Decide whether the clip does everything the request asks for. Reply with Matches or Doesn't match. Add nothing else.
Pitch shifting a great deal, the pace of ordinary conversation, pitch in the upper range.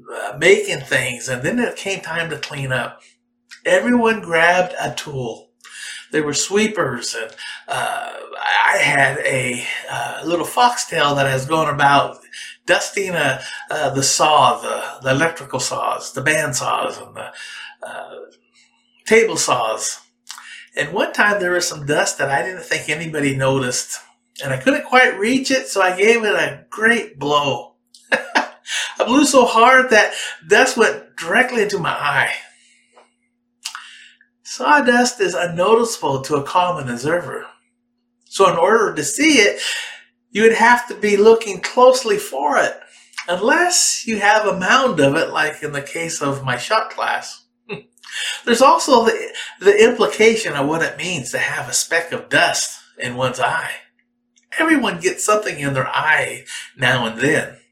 Matches